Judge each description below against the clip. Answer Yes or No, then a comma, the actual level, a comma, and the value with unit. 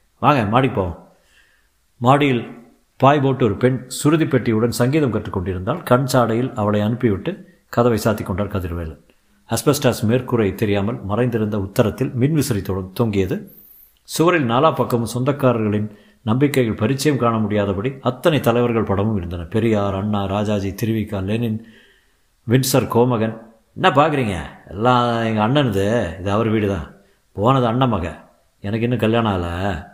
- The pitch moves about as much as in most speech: Yes, average, 3.6 semitones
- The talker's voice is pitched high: No, low, 115 Hz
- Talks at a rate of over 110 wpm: Yes, average, 120 wpm